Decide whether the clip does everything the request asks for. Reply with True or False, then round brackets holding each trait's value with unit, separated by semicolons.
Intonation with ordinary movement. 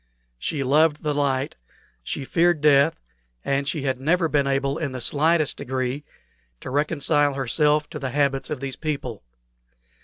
False (2.0 semitones)